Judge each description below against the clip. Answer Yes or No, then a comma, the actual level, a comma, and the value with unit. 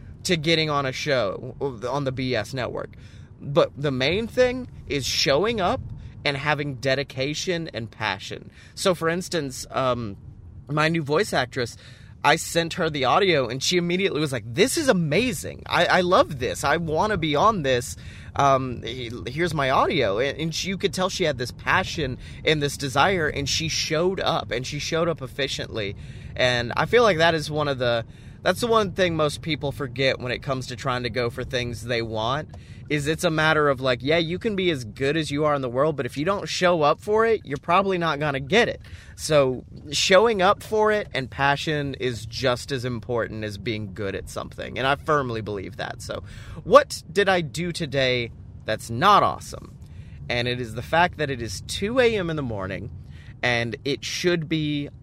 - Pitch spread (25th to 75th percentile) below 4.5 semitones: No, average, 5.0 semitones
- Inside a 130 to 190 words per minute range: No, average, 200 wpm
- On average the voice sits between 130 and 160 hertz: Yes, medium, 140 Hz